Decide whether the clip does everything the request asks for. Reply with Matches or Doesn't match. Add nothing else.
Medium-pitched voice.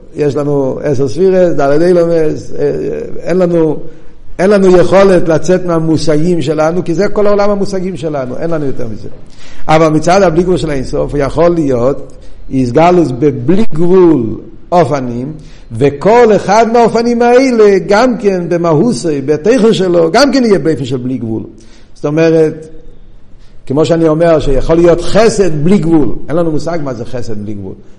Matches